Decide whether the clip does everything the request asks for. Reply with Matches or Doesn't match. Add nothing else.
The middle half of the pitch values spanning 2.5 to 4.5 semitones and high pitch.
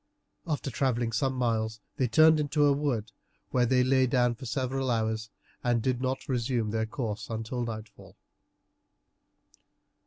Doesn't match